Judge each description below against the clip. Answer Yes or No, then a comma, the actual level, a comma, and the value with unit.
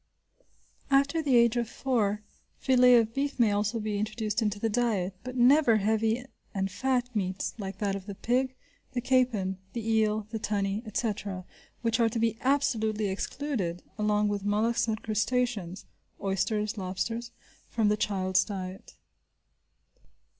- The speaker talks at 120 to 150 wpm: Yes, average, 145 wpm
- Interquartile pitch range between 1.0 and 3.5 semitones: Yes, average, 3.0 semitones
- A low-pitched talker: No, high, 220 Hz